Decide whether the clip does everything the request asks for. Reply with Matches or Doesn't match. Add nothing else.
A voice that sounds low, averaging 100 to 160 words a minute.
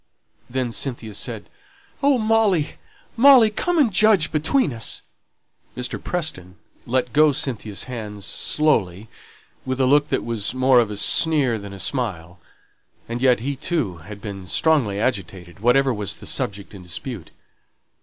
Matches